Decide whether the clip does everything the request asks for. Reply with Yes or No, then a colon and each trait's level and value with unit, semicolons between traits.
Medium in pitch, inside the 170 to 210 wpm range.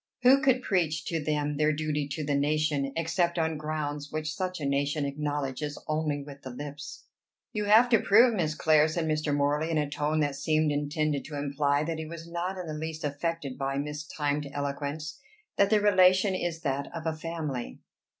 Yes: medium, 155 Hz; average, 190 wpm